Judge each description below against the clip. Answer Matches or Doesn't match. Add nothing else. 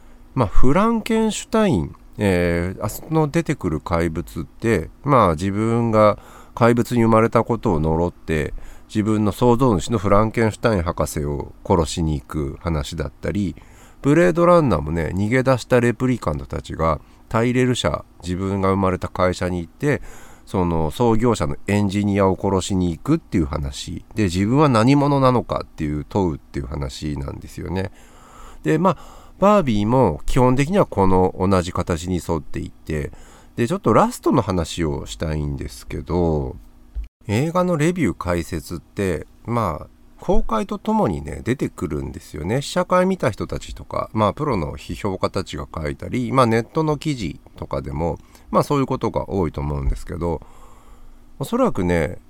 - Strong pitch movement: Matches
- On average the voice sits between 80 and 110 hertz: Matches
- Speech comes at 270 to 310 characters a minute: Doesn't match